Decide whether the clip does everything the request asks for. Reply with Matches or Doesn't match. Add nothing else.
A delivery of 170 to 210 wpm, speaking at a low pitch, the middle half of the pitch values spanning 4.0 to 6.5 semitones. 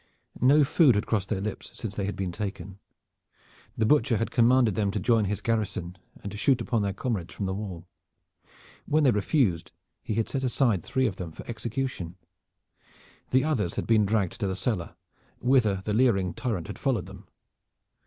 Matches